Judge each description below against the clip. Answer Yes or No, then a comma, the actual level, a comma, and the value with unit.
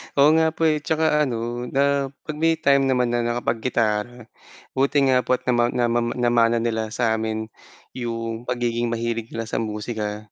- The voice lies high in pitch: No, low, 120 Hz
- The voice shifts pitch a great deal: No, average, 2.7 semitones